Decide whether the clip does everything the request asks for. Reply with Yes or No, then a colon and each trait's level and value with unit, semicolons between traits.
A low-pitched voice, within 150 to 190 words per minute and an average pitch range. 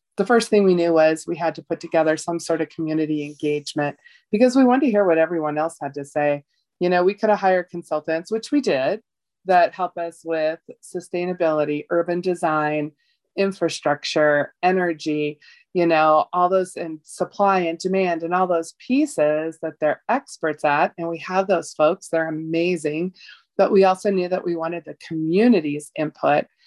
No: medium, 170 Hz; average, 180 wpm; average, 3.1 semitones